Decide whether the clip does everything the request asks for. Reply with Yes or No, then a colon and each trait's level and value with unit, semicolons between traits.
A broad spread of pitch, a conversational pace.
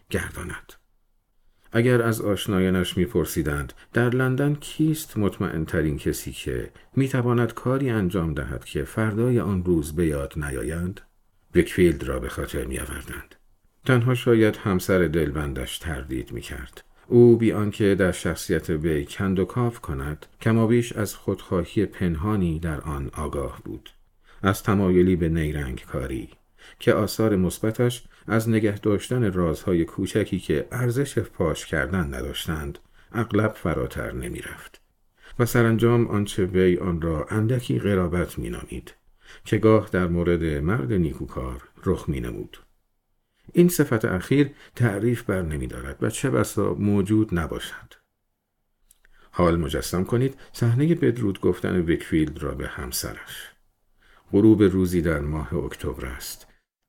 Yes: wide, 6.0 semitones; average, 130 wpm